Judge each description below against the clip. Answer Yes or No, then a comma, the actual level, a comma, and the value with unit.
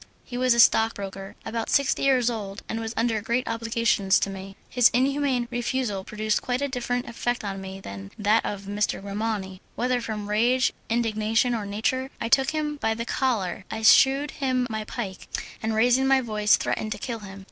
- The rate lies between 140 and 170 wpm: No, average, 190 wpm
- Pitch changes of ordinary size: Yes, average, 3.2 semitones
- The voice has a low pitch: No, high, 225 Hz